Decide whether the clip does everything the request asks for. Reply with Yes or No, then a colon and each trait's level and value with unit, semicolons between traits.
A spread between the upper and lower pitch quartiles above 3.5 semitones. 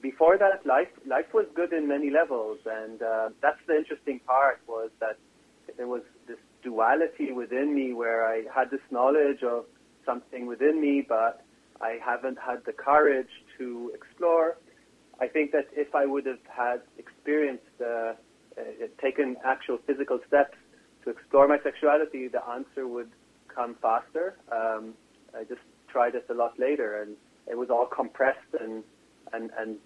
Yes: average, 4.5 semitones